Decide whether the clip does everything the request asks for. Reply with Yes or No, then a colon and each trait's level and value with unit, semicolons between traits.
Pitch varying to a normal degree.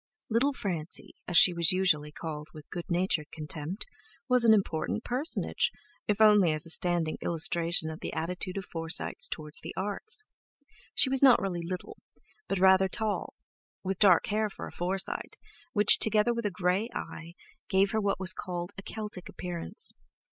Yes: average, 3.8 semitones